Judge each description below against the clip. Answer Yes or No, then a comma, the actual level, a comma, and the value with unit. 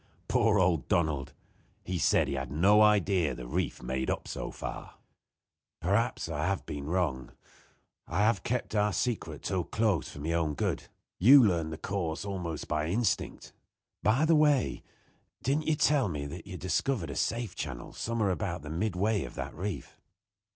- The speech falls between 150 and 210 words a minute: Yes, average, 170 wpm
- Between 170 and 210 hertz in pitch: No, very low, 90 Hz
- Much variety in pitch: Yes, wide, 5.7 semitones